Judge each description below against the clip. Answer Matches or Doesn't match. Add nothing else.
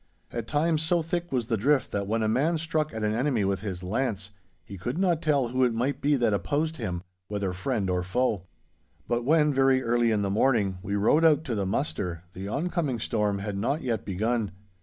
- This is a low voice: Matches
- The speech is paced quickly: Matches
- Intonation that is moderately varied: Doesn't match